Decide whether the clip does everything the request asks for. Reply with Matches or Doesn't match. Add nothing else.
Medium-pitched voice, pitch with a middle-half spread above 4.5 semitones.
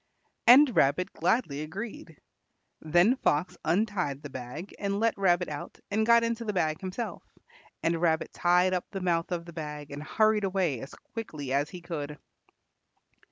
Matches